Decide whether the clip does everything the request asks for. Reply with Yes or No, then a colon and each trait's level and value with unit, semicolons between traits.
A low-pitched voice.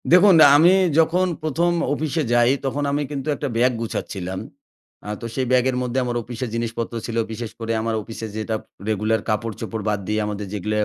Yes: low, 120 Hz